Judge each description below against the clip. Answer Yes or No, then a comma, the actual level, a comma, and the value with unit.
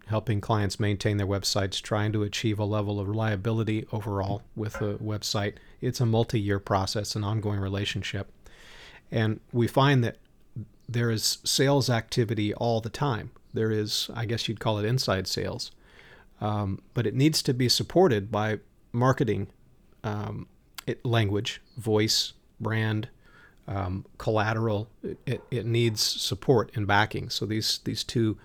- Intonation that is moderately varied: No, narrow, 2.1 semitones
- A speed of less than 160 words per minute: Yes, average, 150 wpm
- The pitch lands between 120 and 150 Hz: No, low, 110 Hz